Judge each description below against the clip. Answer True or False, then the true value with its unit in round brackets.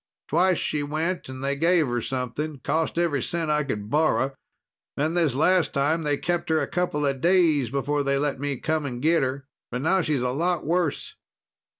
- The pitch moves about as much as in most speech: True (3.3 semitones)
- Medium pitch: True (150 Hz)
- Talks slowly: False (195 wpm)